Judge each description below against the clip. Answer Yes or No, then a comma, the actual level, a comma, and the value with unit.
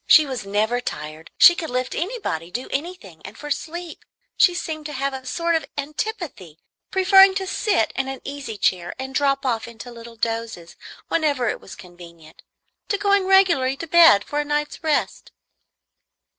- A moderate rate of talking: Yes, average, 170 wpm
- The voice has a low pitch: No, very high, 275 Hz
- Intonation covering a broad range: Yes, wide, 7.0 semitones